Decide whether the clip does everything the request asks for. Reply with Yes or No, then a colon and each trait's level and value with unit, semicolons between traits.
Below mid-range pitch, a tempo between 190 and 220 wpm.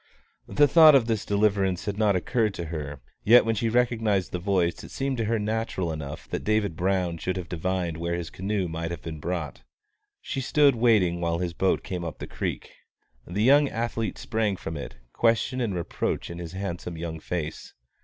Yes: very low, 95 Hz; average, 195 wpm